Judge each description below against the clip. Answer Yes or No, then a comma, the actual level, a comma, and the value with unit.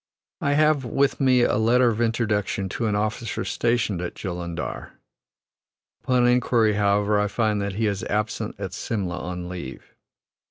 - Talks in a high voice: No, low, 105 Hz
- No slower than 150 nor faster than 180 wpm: Yes, average, 155 wpm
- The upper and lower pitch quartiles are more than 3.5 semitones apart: No, average, 3.0 semitones